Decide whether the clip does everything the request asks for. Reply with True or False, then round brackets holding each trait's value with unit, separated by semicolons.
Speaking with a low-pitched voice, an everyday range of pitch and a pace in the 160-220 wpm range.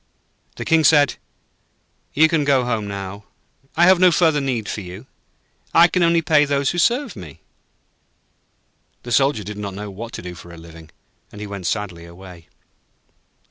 False (115 Hz; 8.6 semitones; 175 wpm)